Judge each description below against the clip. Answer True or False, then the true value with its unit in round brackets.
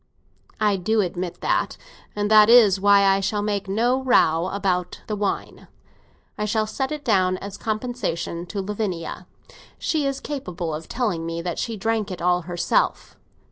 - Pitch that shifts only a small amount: False (3.5 semitones)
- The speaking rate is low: False (165 wpm)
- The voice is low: False (200 Hz)